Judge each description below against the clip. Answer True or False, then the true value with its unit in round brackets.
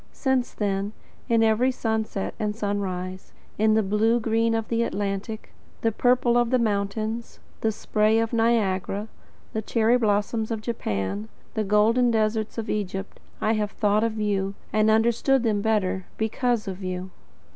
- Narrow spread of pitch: True (2.1 semitones)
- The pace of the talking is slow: False (155 wpm)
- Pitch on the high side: True (215 Hz)